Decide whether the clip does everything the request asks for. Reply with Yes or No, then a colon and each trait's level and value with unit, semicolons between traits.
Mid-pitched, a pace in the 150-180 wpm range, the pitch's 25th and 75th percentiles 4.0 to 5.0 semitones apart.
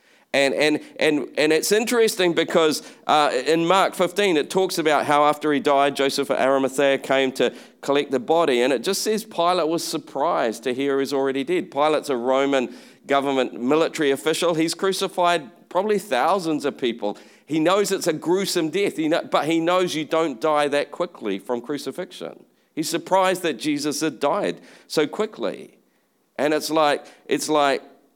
Yes: medium, 155 Hz; average, 170 wpm; average, 4.3 semitones